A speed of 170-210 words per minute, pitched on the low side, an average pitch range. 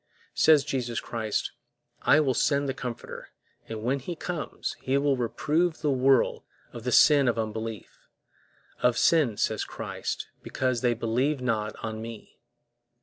No: average, 150 wpm; low, 125 Hz; average, 3.8 semitones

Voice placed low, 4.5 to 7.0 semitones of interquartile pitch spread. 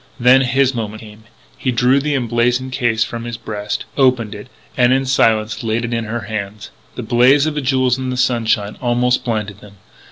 No: low, 120 Hz; average, 2.7 semitones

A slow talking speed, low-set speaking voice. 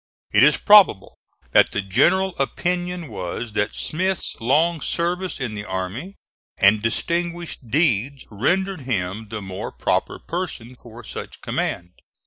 Yes: slow, 130 wpm; low, 130 Hz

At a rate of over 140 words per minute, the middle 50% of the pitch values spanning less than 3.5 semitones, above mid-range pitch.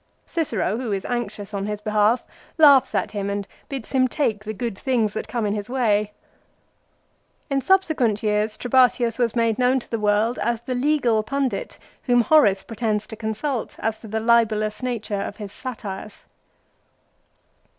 Yes: average, 165 wpm; average, 3.0 semitones; high, 225 Hz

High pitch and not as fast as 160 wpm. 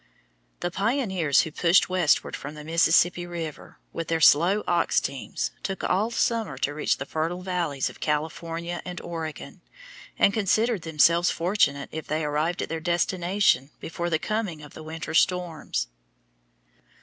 No: medium, 170 Hz; average, 150 wpm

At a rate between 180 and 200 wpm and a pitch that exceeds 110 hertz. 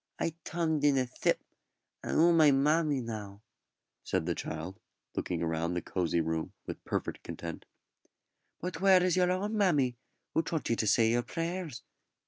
No: average, 165 wpm; low, 135 Hz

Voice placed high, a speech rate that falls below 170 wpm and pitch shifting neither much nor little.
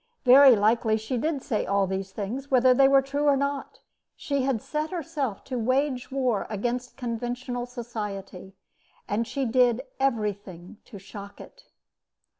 Yes: high, 245 Hz; average, 150 wpm; average, 4.3 semitones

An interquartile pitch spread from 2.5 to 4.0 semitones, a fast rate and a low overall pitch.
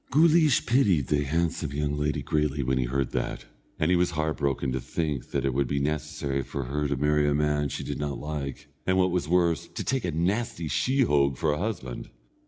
Yes: average, 3.5 semitones; fast, 215 wpm; very low, 75 Hz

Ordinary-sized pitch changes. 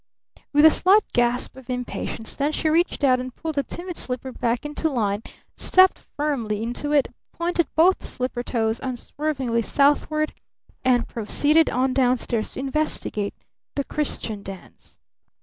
Yes: average, 4.1 semitones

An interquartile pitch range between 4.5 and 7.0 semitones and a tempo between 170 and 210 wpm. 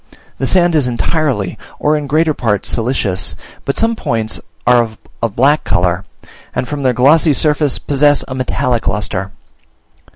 No: average, 4.8 semitones; average, 155 wpm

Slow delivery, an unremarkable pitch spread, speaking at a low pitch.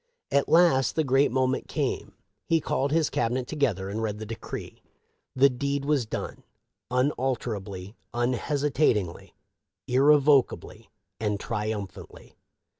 Yes: slow, 115 wpm; average, 4.4 semitones; low, 130 Hz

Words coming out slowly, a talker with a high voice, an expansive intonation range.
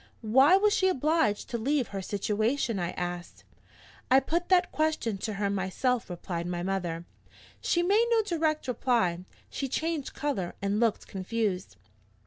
No: average, 150 wpm; high, 230 Hz; wide, 8.2 semitones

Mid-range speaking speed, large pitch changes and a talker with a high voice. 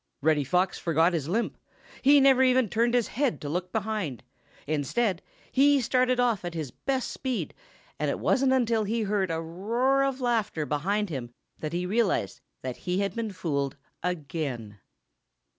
Yes: average, 165 wpm; wide, 7.1 semitones; high, 200 Hz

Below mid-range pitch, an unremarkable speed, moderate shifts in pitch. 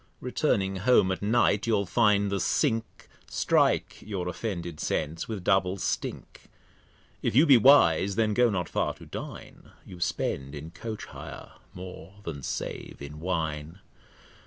Yes: very low, 95 Hz; average, 145 wpm; average, 4.3 semitones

